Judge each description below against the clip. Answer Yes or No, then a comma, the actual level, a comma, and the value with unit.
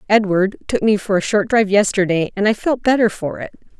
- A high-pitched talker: Yes, high, 205 Hz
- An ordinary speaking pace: No, fast, 220 wpm